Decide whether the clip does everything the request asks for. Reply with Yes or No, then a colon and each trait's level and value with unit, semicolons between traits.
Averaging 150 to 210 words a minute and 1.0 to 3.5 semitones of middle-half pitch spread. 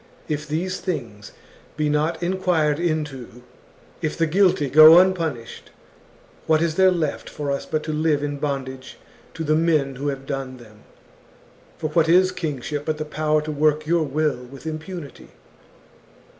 Yes: average, 160 wpm; narrow, 2.6 semitones